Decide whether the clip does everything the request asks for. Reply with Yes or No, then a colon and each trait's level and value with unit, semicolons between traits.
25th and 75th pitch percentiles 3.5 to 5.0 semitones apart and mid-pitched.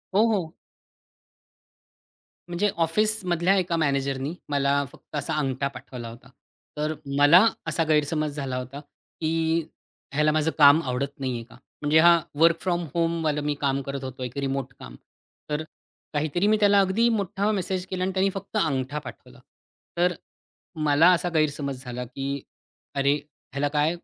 Yes: average, 3.9 semitones; medium, 150 Hz